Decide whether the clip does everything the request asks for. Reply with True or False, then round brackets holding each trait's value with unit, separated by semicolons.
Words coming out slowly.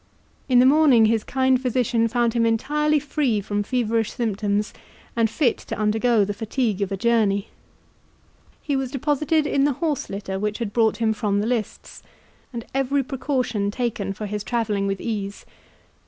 False (170 wpm)